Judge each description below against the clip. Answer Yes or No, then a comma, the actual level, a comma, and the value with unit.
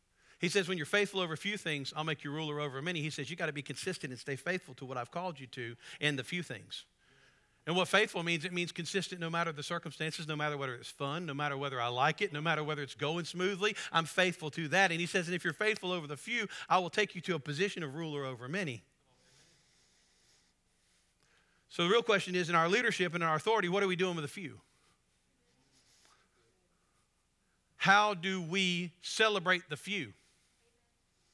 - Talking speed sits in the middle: No, fast, 215 wpm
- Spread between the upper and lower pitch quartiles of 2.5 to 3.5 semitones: No, average, 4.1 semitones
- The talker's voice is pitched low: No, medium, 165 Hz